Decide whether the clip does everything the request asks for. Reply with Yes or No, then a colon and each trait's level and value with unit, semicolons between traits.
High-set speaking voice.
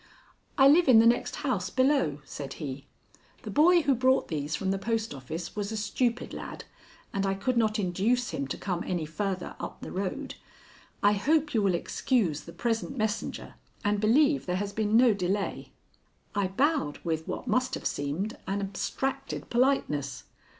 Yes: high, 210 Hz